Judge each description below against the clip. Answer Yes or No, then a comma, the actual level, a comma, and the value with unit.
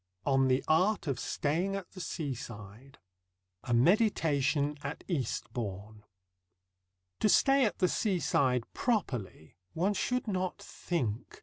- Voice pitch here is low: No, medium, 145 Hz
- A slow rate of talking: Yes, slow, 115 wpm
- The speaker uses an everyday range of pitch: No, wide, 7.4 semitones